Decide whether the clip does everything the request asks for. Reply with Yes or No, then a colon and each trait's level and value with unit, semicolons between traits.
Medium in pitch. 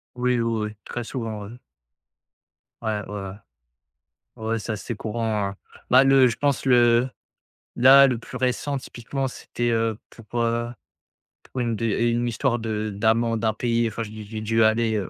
No: low, 115 Hz